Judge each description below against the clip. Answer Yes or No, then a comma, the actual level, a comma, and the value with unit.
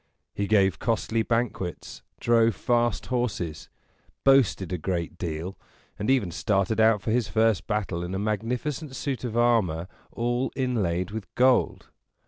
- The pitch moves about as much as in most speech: Yes, average, 4.2 semitones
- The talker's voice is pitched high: No, low, 110 Hz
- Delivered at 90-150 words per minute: Yes, average, 140 wpm